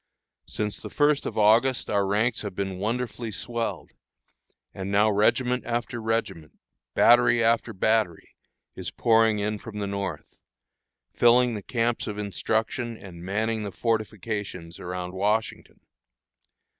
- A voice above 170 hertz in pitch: No, low, 110 Hz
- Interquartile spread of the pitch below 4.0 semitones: Yes, average, 2.7 semitones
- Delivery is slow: Yes, slow, 130 wpm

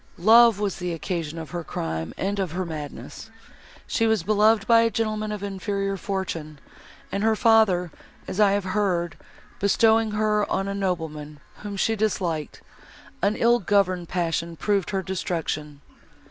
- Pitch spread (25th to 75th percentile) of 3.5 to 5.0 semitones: Yes, average, 3.8 semitones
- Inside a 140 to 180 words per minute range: Yes, average, 155 wpm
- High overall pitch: Yes, high, 195 Hz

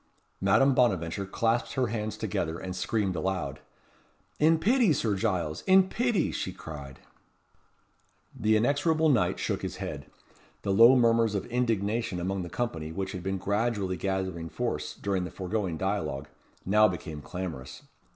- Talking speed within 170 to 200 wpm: No, average, 145 wpm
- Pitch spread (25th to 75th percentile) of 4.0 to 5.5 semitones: Yes, average, 4.5 semitones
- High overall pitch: No, low, 100 Hz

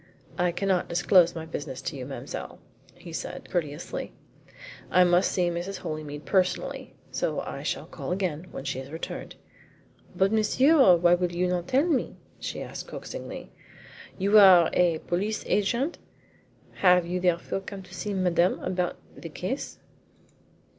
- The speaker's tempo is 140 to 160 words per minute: Yes, average, 150 wpm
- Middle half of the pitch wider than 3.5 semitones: No, narrow, 2.4 semitones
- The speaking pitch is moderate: Yes, medium, 180 Hz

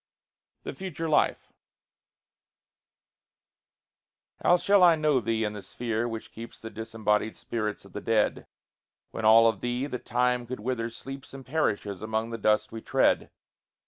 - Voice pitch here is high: No, low, 115 Hz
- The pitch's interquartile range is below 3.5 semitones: Yes, average, 2.9 semitones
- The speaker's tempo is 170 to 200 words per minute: No, average, 150 wpm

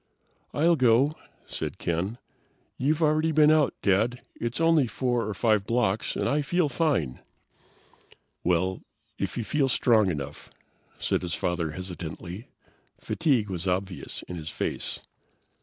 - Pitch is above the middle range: No, low, 115 Hz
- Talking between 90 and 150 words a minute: Yes, slow, 135 wpm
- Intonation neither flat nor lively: No, wide, 8.1 semitones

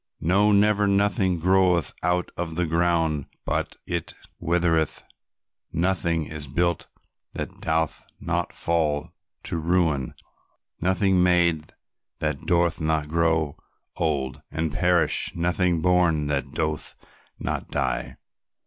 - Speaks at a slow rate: Yes, slow, 110 wpm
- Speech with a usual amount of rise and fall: No, narrow, 2.2 semitones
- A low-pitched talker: Yes, very low, 85 Hz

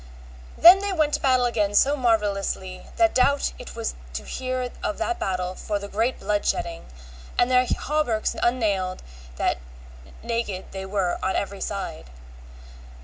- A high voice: Yes, high, 215 Hz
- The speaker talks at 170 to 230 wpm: No, average, 150 wpm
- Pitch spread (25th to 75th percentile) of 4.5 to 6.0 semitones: Yes, average, 5.0 semitones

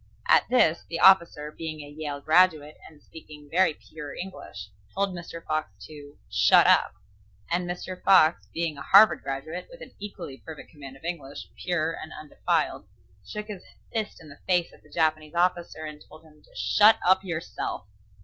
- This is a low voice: No, medium, 160 Hz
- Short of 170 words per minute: No, average, 175 wpm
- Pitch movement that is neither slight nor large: Yes, average, 3.1 semitones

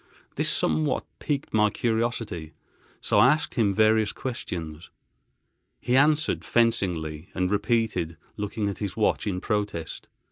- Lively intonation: No, average, 4.7 semitones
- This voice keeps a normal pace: No, slow, 130 wpm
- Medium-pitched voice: No, low, 105 Hz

